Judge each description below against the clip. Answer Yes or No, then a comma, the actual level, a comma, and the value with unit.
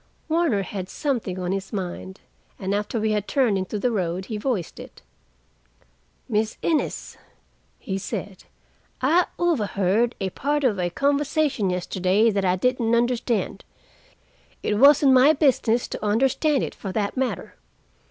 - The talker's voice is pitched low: No, high, 220 Hz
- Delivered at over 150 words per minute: No, average, 145 wpm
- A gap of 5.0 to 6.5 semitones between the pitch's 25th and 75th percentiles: Yes, wide, 5.6 semitones